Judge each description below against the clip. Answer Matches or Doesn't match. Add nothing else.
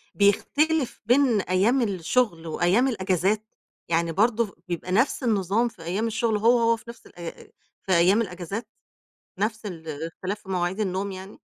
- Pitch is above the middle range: Matches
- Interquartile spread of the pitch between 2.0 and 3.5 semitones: Doesn't match